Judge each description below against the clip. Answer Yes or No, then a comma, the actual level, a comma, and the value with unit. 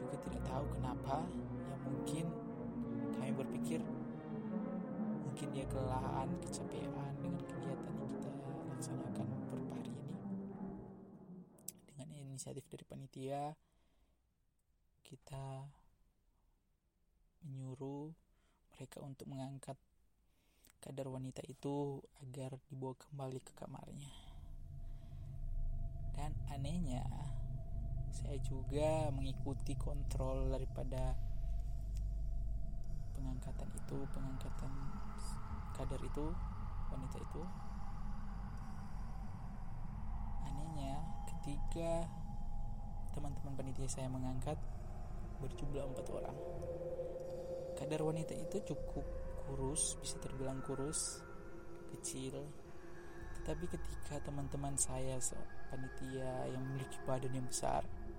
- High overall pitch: No, low, 135 Hz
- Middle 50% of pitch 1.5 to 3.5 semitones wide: Yes, average, 2.8 semitones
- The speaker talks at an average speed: No, slow, 80 wpm